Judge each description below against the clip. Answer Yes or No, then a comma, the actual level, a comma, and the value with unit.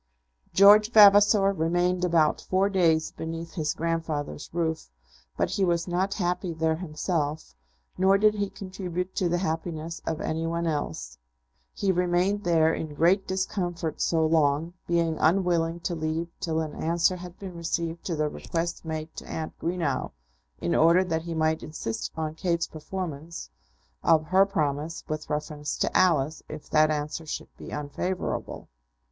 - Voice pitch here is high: No, medium, 165 Hz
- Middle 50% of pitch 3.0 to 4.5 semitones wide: No, narrow, 2.4 semitones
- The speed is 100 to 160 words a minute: Yes, average, 155 wpm